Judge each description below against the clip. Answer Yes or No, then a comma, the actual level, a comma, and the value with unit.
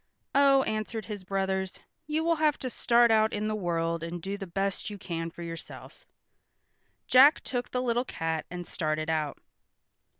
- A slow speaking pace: No, average, 170 wpm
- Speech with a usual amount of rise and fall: No, wide, 6.4 semitones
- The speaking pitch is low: No, high, 200 Hz